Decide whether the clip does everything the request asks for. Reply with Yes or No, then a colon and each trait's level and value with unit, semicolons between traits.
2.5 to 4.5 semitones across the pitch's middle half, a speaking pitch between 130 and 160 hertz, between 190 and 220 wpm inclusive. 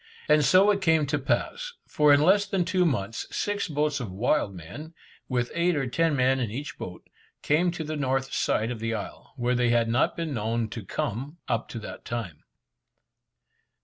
No: wide, 5.6 semitones; low, 135 Hz; average, 195 wpm